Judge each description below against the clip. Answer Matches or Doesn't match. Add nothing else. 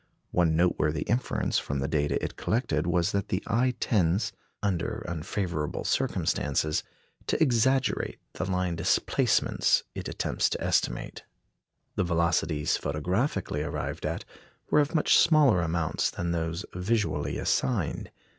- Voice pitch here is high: Doesn't match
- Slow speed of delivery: Matches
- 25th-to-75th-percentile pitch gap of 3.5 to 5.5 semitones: Matches